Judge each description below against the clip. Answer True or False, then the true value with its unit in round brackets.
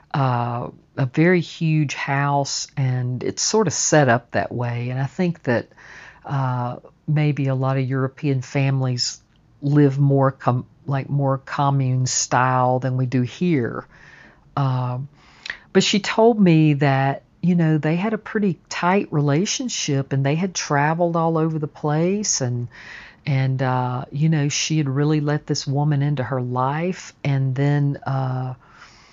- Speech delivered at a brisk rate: False (150 wpm)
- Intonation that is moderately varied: True (3.1 semitones)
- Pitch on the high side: False (140 Hz)